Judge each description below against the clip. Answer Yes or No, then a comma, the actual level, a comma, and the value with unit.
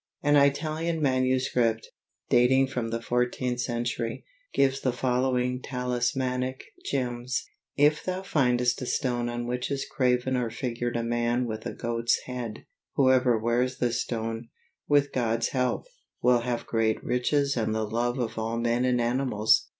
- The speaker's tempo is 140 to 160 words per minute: Yes, average, 150 wpm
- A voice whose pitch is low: Yes, low, 125 Hz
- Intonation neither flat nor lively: No, narrow, 1.7 semitones